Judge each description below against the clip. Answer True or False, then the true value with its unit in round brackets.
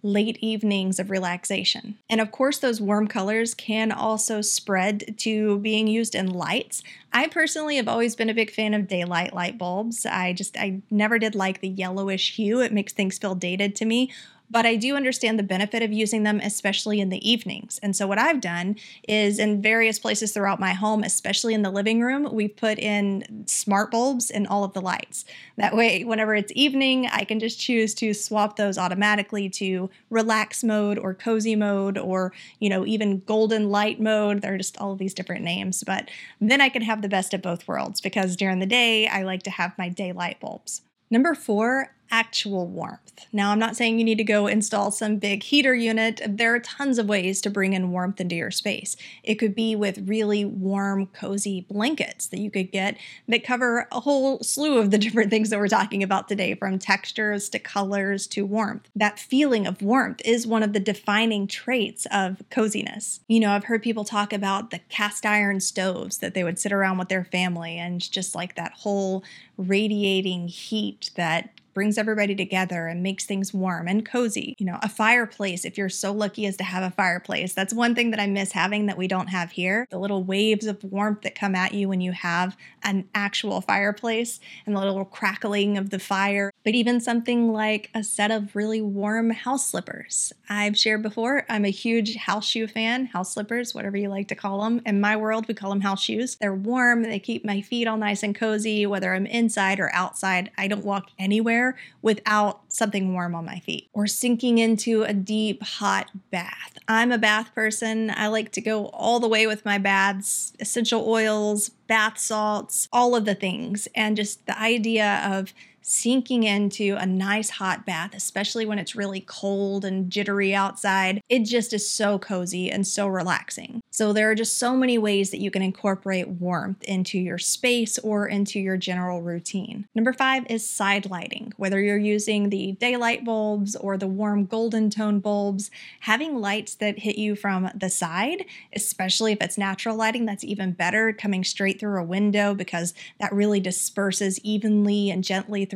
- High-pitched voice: True (205 Hz)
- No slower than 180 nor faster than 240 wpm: True (200 wpm)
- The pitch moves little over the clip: True (2.3 semitones)